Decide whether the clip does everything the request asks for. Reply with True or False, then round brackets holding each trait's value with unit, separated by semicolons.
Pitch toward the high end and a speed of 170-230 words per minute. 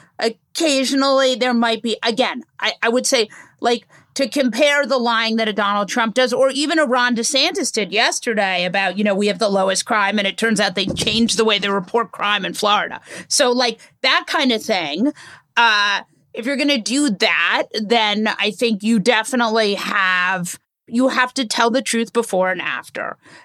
True (230 Hz; 190 wpm)